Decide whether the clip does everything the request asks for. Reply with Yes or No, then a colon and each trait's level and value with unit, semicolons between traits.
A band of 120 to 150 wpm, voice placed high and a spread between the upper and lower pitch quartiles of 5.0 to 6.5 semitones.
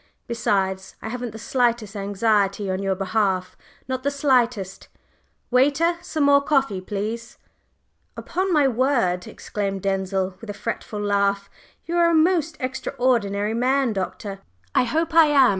Yes: average, 140 wpm; high, 230 Hz; wide, 5.6 semitones